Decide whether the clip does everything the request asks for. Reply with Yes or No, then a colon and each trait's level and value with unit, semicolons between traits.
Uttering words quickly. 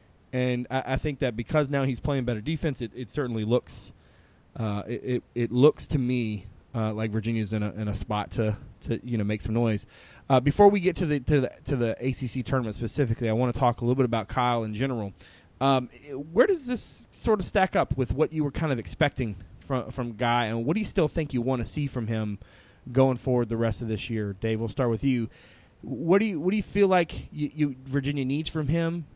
Yes: fast, 235 wpm